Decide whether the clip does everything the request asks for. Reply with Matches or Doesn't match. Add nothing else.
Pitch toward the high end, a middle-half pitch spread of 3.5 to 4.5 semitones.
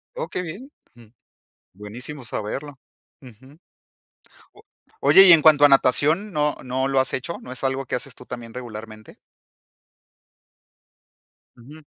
Doesn't match